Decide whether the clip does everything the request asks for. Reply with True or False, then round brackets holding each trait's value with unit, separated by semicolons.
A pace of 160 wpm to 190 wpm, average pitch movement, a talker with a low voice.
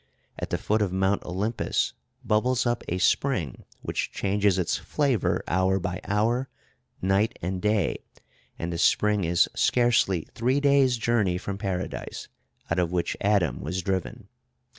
False (145 wpm; 4.0 semitones; 100 Hz)